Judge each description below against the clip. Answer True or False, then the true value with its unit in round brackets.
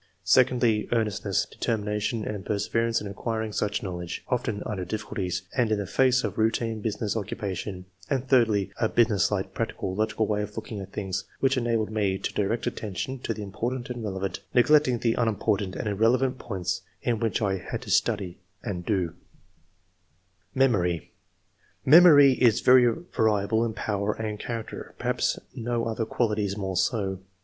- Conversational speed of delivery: True (165 wpm)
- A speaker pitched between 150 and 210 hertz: False (110 Hz)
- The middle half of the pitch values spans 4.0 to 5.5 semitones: False (3.0 semitones)